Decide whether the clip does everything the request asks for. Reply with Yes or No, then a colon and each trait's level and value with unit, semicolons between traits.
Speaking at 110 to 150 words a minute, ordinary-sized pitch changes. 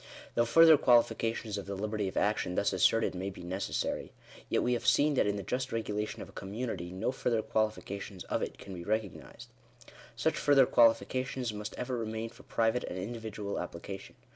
No: average, 200 wpm; average, 3.3 semitones